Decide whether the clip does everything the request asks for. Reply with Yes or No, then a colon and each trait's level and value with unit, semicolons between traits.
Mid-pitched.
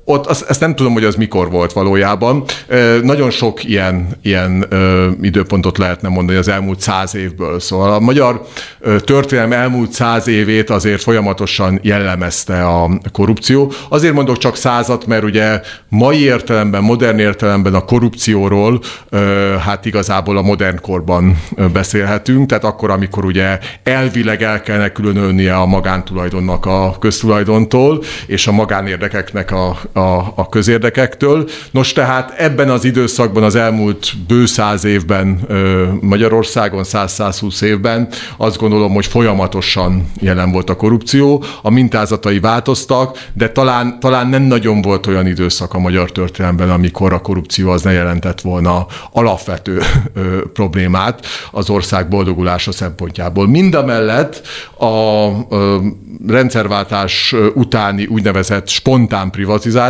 No: low, 105 Hz